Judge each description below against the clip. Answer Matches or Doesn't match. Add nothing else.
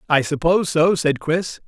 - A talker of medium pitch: Matches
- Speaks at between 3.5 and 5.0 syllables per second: Matches